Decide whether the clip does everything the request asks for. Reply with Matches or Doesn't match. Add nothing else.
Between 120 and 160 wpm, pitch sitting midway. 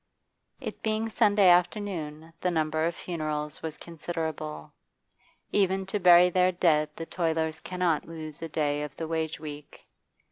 Matches